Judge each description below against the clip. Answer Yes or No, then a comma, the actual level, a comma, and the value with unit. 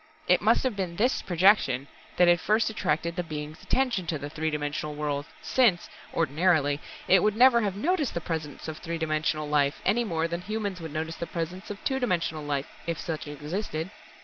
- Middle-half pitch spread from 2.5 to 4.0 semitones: No, average, 4.6 semitones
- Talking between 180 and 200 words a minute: Yes, average, 195 wpm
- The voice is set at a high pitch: No, medium, 170 Hz